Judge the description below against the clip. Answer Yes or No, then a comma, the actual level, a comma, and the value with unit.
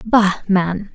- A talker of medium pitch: No, high, 195 Hz